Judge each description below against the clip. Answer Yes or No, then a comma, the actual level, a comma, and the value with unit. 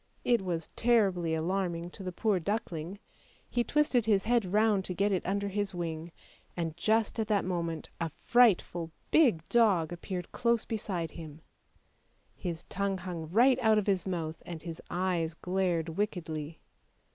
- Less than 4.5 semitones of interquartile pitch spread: Yes, average, 4.1 semitones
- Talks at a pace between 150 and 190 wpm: Yes, average, 155 wpm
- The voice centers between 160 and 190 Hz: Yes, medium, 185 Hz